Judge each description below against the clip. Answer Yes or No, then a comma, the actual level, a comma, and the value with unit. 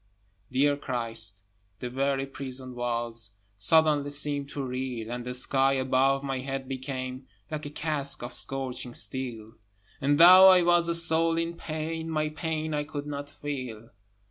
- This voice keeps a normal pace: Yes, average, 155 wpm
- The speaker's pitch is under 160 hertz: Yes, low, 135 Hz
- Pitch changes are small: No, average, 3.2 semitones